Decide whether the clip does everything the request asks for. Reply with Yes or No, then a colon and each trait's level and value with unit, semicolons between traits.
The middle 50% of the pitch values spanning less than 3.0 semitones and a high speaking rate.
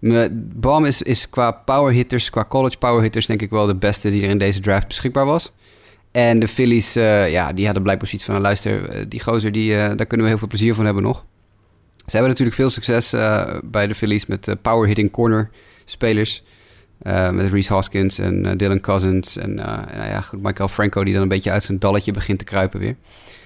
Yes: narrow, 2.6 semitones; fast, 225 wpm